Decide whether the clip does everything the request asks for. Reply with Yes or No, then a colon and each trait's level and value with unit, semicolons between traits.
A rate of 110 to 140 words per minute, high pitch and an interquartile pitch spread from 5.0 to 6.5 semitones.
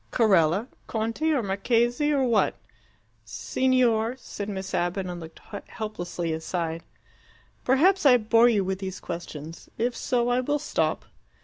Yes: slow, 135 wpm; high, 220 Hz; average, 5.3 semitones